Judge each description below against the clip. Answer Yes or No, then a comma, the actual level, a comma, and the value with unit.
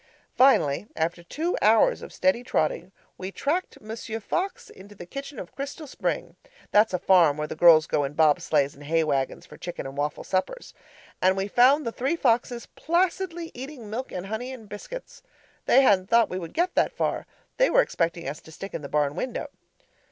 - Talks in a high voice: Yes, high, 205 Hz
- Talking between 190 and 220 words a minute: Yes, average, 195 wpm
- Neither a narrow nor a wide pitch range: No, wide, 8.7 semitones